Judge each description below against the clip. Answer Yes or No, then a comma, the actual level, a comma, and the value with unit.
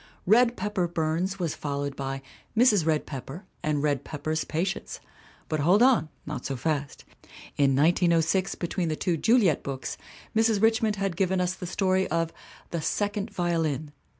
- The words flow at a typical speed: Yes, average, 155 wpm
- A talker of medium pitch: Yes, medium, 170 Hz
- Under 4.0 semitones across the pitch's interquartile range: No, average, 4.3 semitones